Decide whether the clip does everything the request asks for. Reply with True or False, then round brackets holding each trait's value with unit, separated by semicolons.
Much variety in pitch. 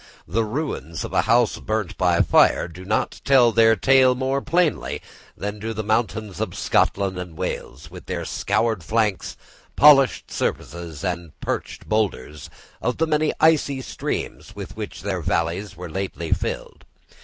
True (6.0 semitones)